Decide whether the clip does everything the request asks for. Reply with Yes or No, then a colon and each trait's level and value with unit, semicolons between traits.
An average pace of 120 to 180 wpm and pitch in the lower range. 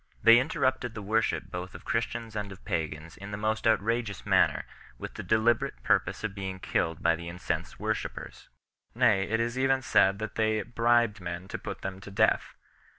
No: average, 190 wpm; low, 105 Hz